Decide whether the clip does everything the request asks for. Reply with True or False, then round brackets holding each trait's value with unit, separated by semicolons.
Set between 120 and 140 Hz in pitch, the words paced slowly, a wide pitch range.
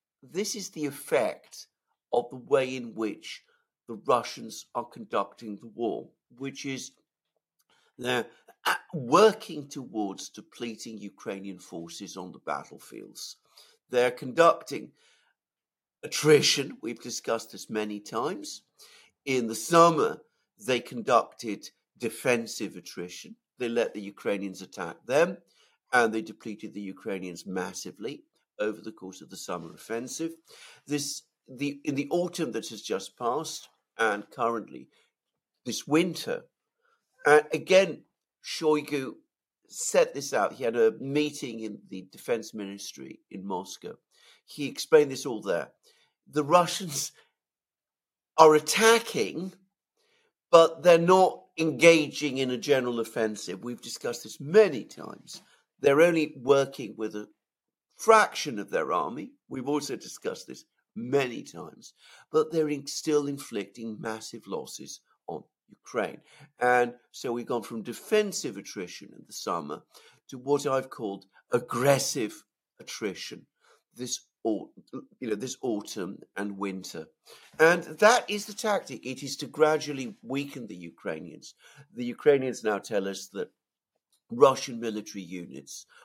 True (135 Hz; 125 wpm; 7.0 semitones)